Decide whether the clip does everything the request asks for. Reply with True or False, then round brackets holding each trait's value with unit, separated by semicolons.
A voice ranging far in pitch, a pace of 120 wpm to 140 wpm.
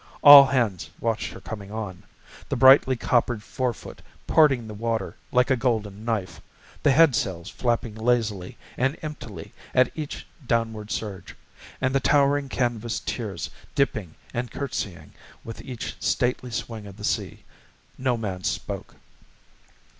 False (3.5 semitones; 135 wpm)